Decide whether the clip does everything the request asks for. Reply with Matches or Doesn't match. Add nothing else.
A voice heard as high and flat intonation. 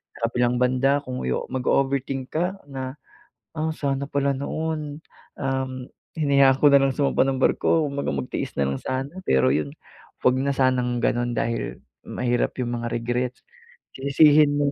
Doesn't match